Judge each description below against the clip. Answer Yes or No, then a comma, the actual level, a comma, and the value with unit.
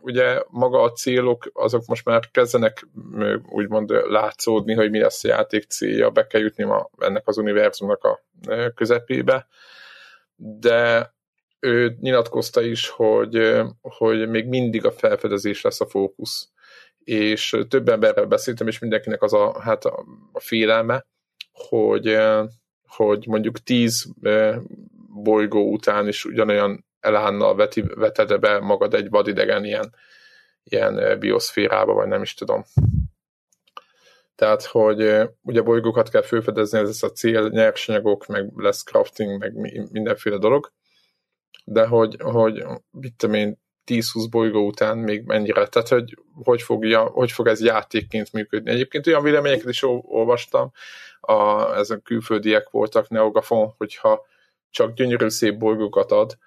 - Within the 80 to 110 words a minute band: No, average, 130 wpm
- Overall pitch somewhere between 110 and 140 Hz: Yes, low, 120 Hz